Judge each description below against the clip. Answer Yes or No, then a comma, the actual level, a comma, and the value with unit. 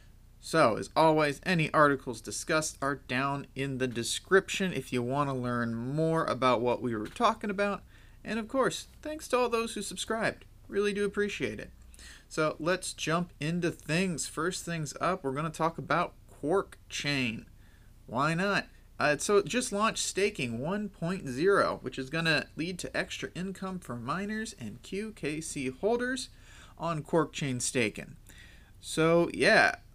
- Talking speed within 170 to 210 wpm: No, average, 160 wpm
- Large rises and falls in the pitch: Yes, wide, 6.9 semitones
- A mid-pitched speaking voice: Yes, medium, 155 Hz